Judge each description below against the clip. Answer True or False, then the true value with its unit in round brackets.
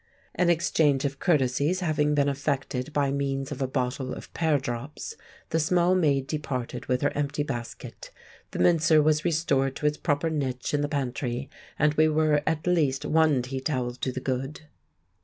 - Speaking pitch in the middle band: True (145 Hz)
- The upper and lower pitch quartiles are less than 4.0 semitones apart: True (2.8 semitones)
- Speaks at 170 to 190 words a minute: True (175 wpm)